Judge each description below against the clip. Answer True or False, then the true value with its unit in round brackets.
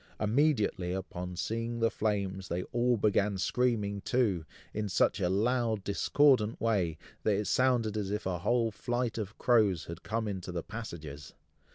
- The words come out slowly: False (160 wpm)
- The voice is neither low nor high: False (105 Hz)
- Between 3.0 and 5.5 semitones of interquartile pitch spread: True (3.6 semitones)